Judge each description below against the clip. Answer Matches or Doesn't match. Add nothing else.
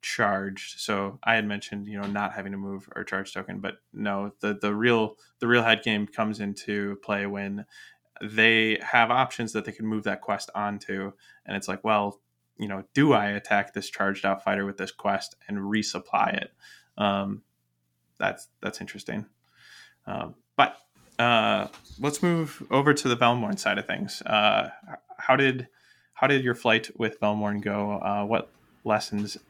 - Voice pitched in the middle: Doesn't match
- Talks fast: Doesn't match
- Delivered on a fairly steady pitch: Matches